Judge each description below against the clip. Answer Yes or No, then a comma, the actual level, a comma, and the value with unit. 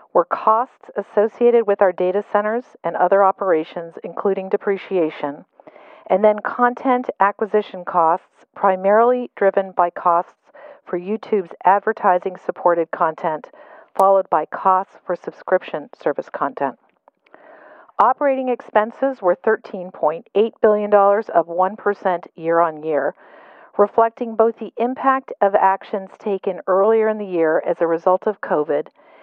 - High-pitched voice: Yes, high, 200 Hz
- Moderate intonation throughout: Yes, average, 3.4 semitones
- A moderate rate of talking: No, slow, 120 wpm